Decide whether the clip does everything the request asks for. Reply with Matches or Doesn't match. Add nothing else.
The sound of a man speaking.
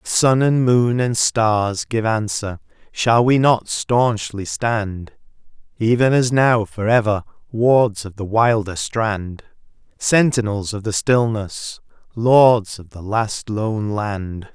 Matches